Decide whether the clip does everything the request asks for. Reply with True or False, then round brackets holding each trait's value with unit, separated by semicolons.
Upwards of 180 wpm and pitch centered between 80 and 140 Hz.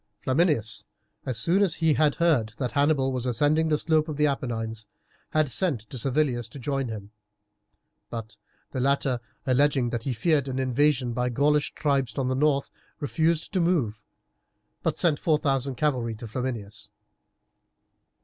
False (160 wpm; 135 Hz)